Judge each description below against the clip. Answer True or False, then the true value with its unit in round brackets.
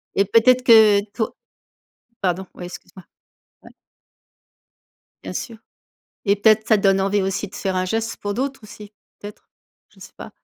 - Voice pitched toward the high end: True (205 Hz)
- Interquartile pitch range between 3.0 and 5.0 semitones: False (2.4 semitones)